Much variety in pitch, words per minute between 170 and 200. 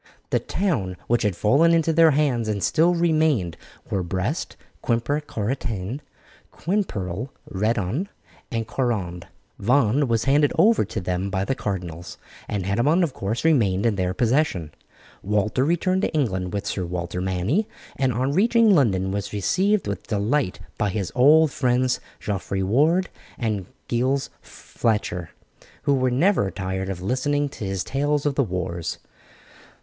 No: wide, 7.3 semitones; average, 145 wpm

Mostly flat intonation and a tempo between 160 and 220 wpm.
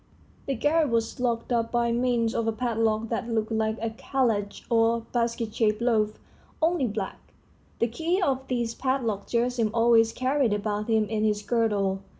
Yes: narrow, 2.1 semitones; average, 165 wpm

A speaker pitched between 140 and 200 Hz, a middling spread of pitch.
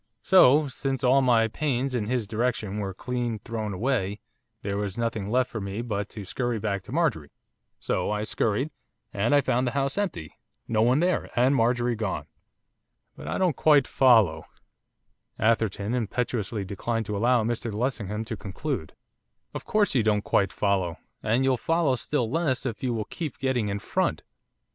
No: low, 115 Hz; average, 3.8 semitones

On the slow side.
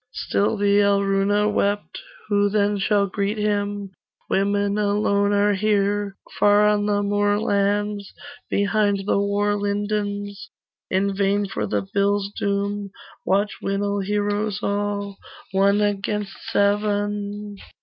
Yes: slow, 115 wpm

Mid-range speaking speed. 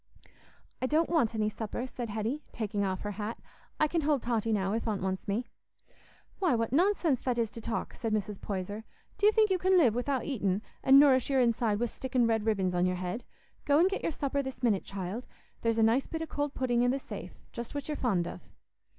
No: fast, 225 wpm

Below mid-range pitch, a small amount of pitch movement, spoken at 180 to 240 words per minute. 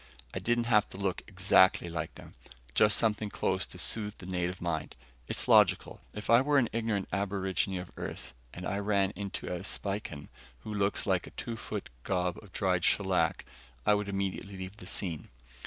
Yes: low, 100 Hz; narrow, 2.3 semitones; average, 185 wpm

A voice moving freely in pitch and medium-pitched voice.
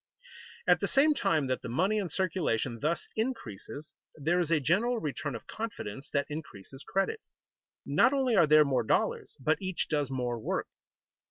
Yes: wide, 6.6 semitones; medium, 155 Hz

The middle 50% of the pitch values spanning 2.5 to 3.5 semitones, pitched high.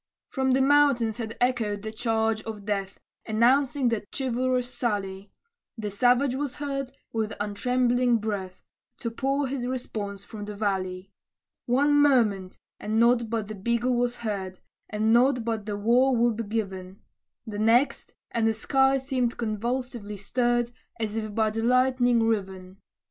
Yes: average, 3.2 semitones; high, 230 Hz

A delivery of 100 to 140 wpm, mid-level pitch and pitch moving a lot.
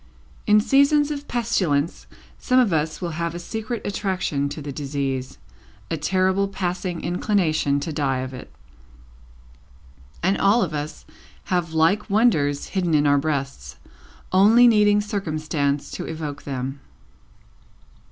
Yes: slow, 135 wpm; medium, 170 Hz; wide, 5.9 semitones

